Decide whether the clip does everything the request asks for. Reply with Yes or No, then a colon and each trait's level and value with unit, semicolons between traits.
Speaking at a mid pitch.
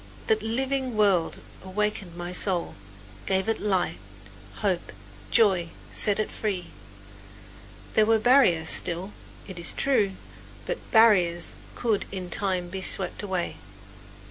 No: high, 195 Hz